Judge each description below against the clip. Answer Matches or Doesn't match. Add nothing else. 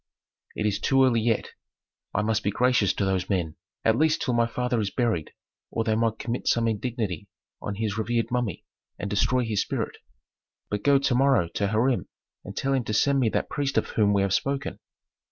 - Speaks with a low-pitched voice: Matches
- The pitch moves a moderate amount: Matches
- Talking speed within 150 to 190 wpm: Doesn't match